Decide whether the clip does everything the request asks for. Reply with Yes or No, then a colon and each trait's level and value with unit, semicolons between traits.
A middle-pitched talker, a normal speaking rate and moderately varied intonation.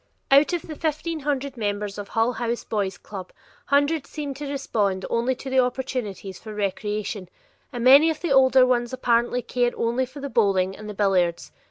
No: high, 245 Hz; average, 190 wpm; average, 4.7 semitones